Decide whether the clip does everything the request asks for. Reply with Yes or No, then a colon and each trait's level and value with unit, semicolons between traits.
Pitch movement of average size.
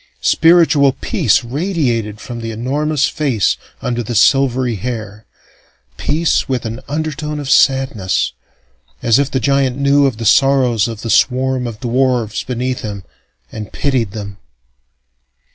Yes: average, 3.5 semitones